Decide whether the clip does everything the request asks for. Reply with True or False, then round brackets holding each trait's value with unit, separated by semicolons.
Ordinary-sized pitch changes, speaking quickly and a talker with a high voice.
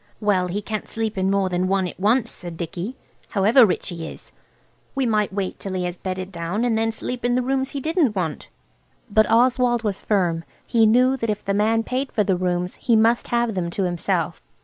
True (4.3 semitones; 215 wpm; 210 Hz)